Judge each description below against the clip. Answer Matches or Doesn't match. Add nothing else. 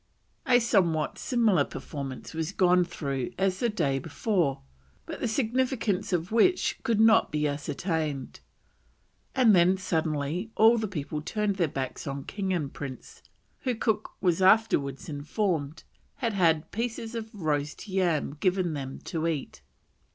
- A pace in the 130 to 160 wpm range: Matches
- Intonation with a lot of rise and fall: Matches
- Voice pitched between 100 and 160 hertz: Doesn't match